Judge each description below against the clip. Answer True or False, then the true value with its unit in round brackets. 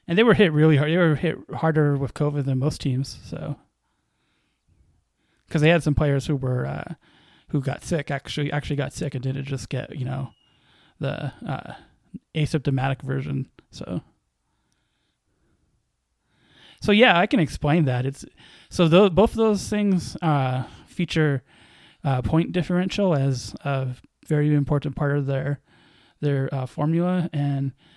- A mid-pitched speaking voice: True (145 Hz)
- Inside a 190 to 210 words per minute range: False (150 wpm)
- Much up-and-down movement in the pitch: False (3.3 semitones)